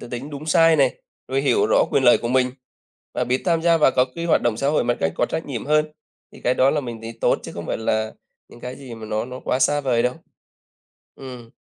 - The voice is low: Yes, low, 130 Hz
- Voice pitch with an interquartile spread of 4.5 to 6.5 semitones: No, average, 3.5 semitones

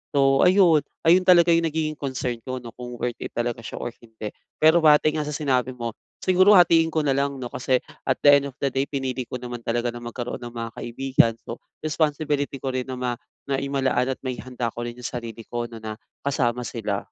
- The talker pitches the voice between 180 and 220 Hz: No, low, 130 Hz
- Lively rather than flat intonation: No, average, 3.7 semitones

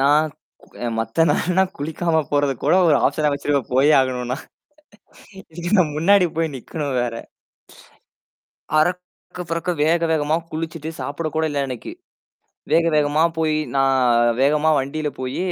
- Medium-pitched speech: Yes, medium, 155 Hz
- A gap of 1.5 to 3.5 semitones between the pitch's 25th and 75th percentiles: Yes, average, 2.9 semitones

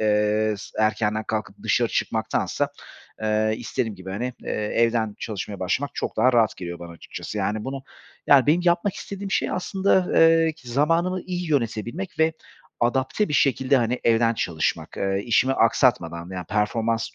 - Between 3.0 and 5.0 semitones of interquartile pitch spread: No, wide, 5.5 semitones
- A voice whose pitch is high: No, low, 115 Hz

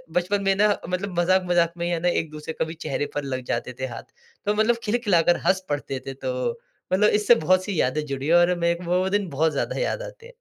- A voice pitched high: No, medium, 175 Hz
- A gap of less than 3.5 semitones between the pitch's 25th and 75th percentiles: No, average, 4.4 semitones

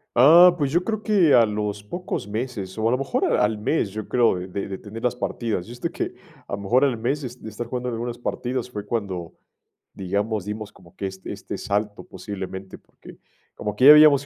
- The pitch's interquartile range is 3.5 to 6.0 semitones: Yes, average, 3.9 semitones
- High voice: No, low, 110 Hz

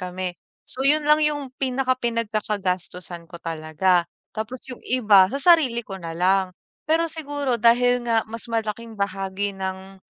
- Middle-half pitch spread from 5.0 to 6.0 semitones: Yes, average, 5.3 semitones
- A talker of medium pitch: No, high, 215 Hz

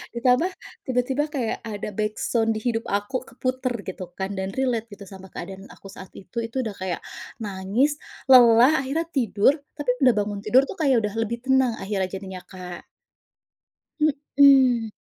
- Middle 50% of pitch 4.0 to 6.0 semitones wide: Yes, average, 4.7 semitones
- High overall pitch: Yes, high, 230 Hz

